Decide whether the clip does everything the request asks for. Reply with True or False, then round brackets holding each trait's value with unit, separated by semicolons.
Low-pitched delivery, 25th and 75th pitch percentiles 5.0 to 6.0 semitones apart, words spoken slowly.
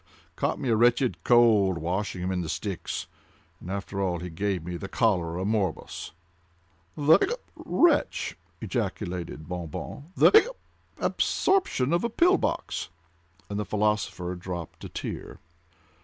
True (95 Hz; 5.4 semitones; 120 wpm)